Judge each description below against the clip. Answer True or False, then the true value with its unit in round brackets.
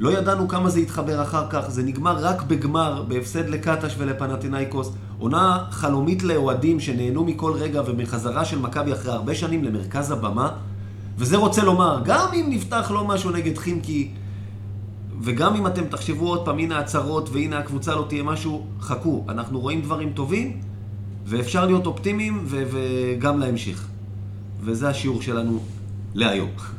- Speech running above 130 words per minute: True (150 wpm)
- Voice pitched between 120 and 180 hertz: True (135 Hz)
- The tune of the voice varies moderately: False (7.2 semitones)